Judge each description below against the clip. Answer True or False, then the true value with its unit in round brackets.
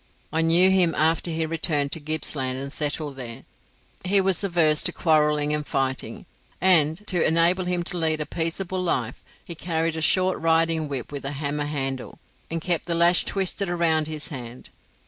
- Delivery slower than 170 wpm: False (180 wpm)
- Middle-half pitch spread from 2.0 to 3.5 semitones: True (2.9 semitones)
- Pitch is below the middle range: False (160 Hz)